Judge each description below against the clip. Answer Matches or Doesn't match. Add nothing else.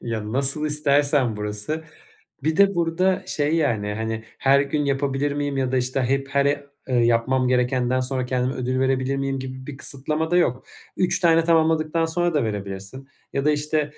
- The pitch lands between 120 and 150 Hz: Matches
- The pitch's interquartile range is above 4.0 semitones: Doesn't match